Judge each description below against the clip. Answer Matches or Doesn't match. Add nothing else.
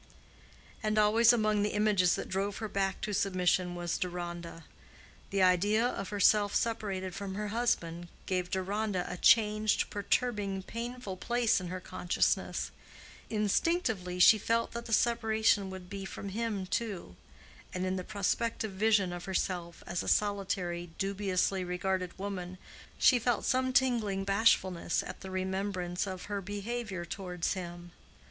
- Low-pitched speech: Doesn't match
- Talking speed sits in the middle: Matches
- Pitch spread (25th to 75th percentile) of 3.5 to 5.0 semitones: Doesn't match